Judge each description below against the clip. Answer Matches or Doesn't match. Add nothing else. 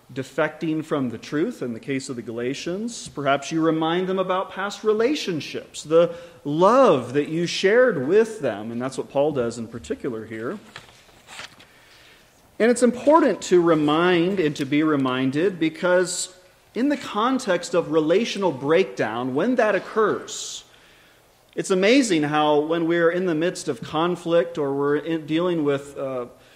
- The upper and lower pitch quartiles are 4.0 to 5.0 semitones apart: Matches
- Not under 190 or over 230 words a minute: Doesn't match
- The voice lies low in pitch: Doesn't match